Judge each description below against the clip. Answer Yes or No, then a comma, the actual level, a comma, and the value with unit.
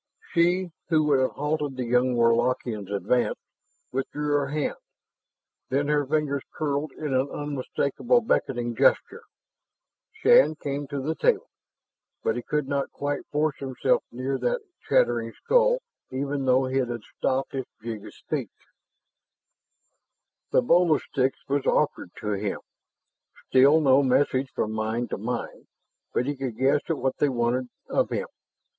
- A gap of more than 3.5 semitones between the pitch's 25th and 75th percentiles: No, average, 2.9 semitones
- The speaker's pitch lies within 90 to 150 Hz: Yes, low, 135 Hz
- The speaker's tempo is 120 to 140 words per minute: No, average, 150 wpm